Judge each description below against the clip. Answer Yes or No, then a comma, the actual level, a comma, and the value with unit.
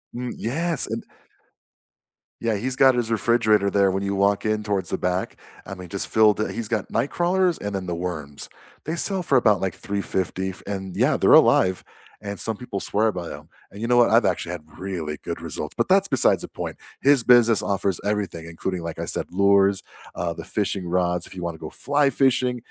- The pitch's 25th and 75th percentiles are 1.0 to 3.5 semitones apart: No, average, 4.6 semitones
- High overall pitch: No, low, 100 Hz